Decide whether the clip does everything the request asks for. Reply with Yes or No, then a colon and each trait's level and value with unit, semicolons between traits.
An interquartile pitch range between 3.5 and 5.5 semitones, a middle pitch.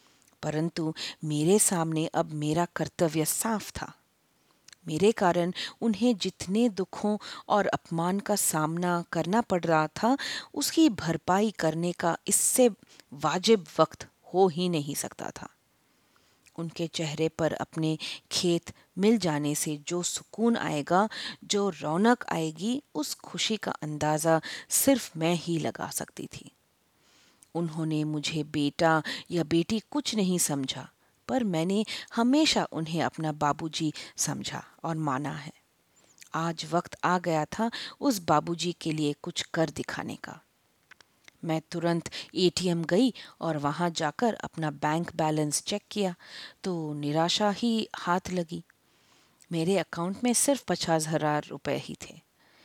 Yes: average, 4.5 semitones; medium, 170 Hz